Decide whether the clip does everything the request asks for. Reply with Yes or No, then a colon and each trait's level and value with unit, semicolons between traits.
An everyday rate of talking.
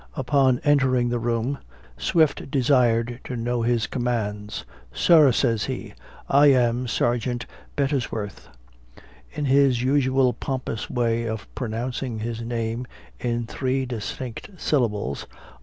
No: slow, 125 wpm